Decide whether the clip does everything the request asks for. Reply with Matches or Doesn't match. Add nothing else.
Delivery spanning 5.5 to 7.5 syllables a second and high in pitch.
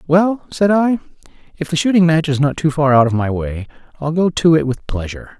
Doesn't match